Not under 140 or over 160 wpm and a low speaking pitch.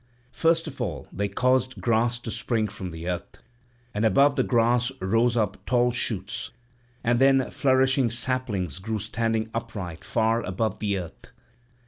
Yes: average, 150 wpm; low, 115 Hz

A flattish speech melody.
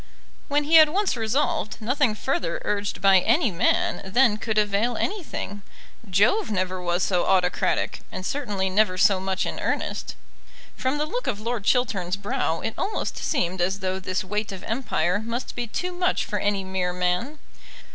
No: wide, 5.4 semitones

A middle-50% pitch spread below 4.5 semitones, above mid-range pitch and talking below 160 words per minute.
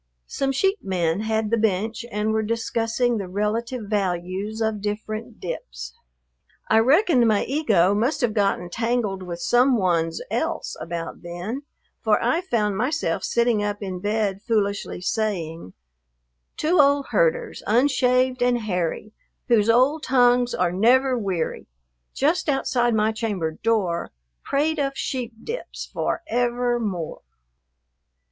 Yes: average, 4.1 semitones; high, 220 Hz; slow, 135 wpm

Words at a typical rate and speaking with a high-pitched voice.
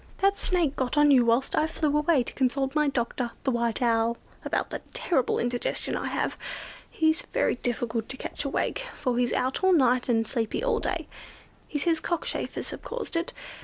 Yes: average, 190 wpm; very high, 265 Hz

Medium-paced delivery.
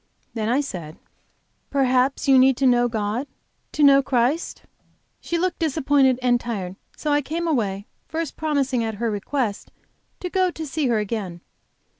Yes: average, 160 wpm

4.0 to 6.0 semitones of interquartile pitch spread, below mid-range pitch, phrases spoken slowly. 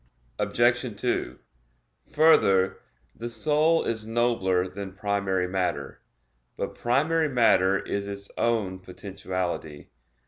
Yes: average, 4.3 semitones; low, 100 Hz; slow, 100 wpm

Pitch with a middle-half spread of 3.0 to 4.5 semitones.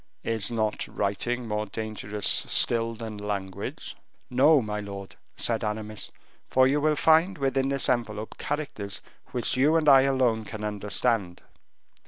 Yes: average, 4.1 semitones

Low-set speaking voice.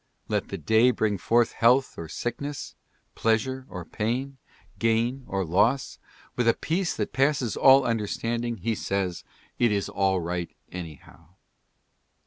Yes: low, 115 Hz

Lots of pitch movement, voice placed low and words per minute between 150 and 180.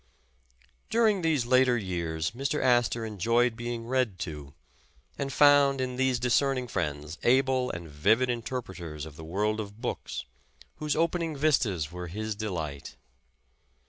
No: wide, 6.8 semitones; low, 120 Hz; slow, 135 wpm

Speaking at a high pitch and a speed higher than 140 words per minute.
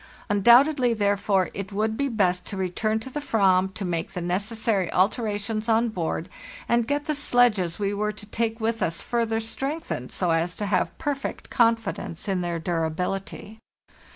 Yes: high, 210 Hz; average, 170 wpm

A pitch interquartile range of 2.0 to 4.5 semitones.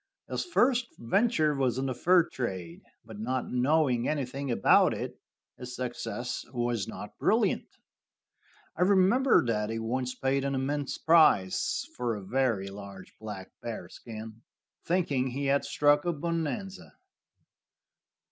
No: average, 5.1 semitones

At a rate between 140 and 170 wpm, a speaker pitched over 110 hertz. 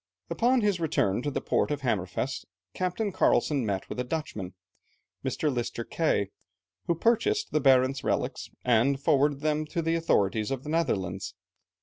Yes: average, 155 wpm; medium, 140 Hz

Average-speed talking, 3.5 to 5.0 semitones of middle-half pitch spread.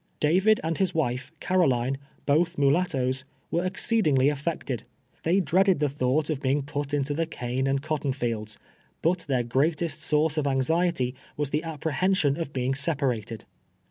Yes: average, 165 wpm; average, 3.8 semitones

